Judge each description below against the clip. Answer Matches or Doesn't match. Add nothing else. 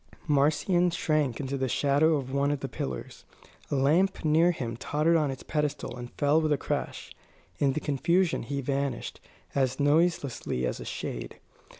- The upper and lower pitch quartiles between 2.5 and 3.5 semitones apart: Matches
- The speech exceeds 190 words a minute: Doesn't match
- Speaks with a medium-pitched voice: Matches